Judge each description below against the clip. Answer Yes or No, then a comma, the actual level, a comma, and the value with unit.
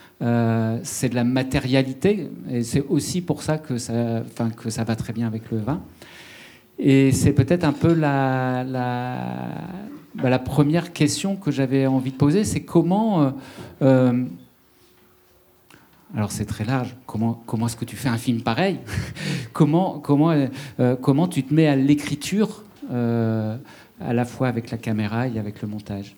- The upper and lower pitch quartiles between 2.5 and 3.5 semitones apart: No, average, 4.1 semitones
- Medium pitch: No, low, 130 Hz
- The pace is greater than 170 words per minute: No, average, 165 wpm